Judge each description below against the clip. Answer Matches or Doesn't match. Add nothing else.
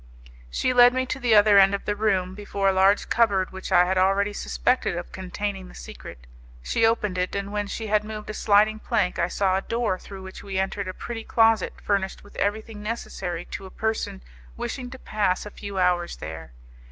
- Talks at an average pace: Doesn't match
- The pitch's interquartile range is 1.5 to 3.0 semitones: Matches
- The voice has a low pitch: Doesn't match